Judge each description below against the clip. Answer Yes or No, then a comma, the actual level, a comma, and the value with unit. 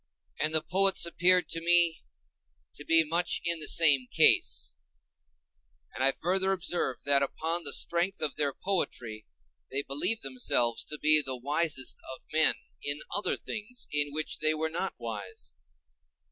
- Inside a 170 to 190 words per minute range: No, average, 155 wpm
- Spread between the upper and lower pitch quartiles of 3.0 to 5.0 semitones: Yes, average, 3.8 semitones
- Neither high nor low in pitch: Yes, medium, 155 Hz